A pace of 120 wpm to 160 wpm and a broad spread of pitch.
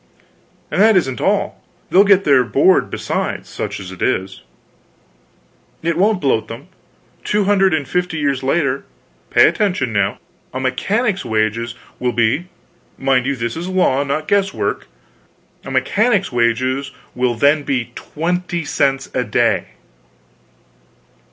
Yes: slow, 135 wpm; wide, 6.6 semitones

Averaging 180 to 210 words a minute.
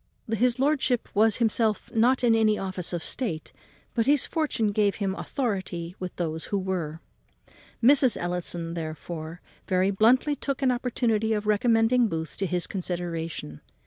No: average, 150 wpm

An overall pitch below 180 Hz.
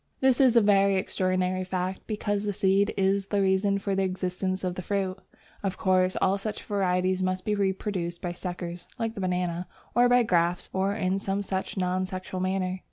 No: high, 190 Hz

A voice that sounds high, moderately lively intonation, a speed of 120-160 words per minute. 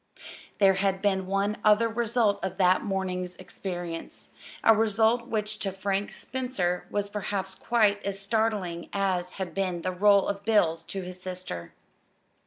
No: high, 195 Hz; narrow, 2.3 semitones; average, 150 wpm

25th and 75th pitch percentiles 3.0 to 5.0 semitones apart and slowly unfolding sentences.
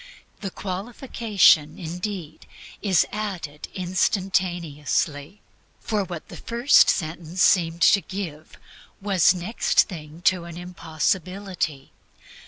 Yes: average, 3.5 semitones; slow, 95 wpm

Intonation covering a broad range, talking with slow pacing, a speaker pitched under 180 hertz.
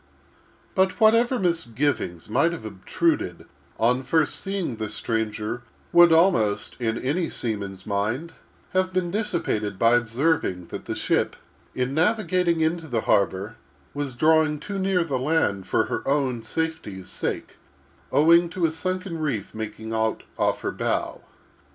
Yes: wide, 7.4 semitones; slow, 120 wpm; medium, 140 Hz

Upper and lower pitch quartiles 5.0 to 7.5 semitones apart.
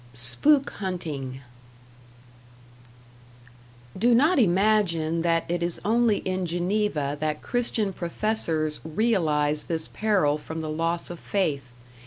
Yes: average, 5.3 semitones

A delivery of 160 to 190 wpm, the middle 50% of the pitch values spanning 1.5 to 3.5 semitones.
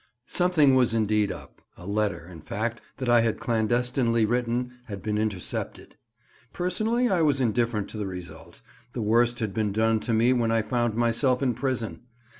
Yes: average, 175 wpm; average, 2.7 semitones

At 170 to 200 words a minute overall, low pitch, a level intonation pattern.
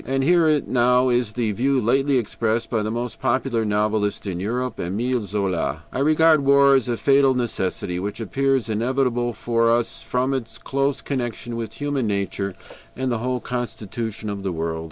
No: average, 175 wpm; low, 120 Hz; average, 3.6 semitones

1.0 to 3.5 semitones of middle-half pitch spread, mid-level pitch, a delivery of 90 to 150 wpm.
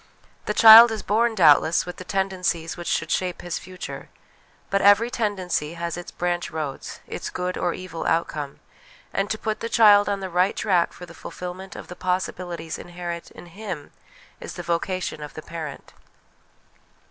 No: average, 2.8 semitones; medium, 180 Hz; average, 175 wpm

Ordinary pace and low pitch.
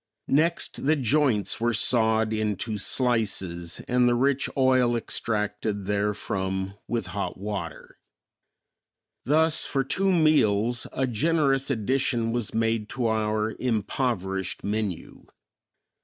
No: slow, 110 wpm; low, 115 Hz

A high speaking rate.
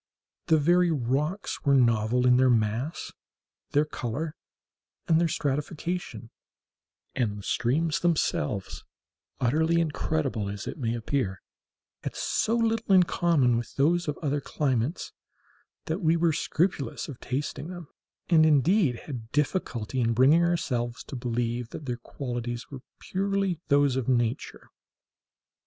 No: slow, 135 wpm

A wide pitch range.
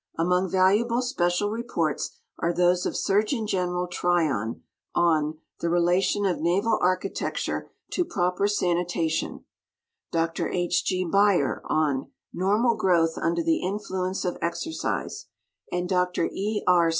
No: narrow, 2.6 semitones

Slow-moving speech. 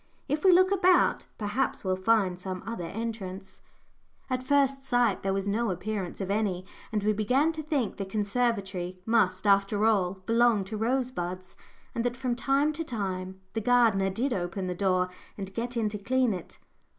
No: average, 175 wpm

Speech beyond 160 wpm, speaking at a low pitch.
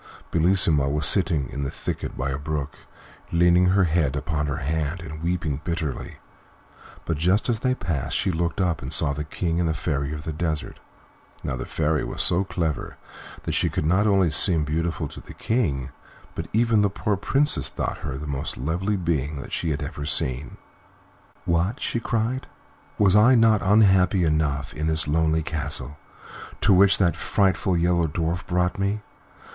Yes: average, 180 wpm; very low, 85 Hz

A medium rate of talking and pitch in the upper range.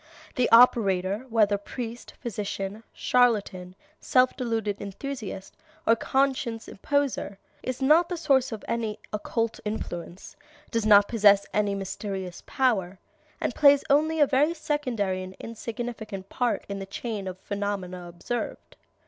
No: slow, 130 wpm; high, 220 Hz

